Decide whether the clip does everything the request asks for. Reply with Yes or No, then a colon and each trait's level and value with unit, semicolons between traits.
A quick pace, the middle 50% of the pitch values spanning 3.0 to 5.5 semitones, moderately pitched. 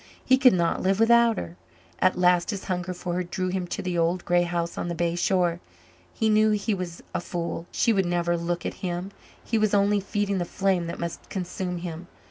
No: fast, 220 wpm; narrow, 2.4 semitones; medium, 180 Hz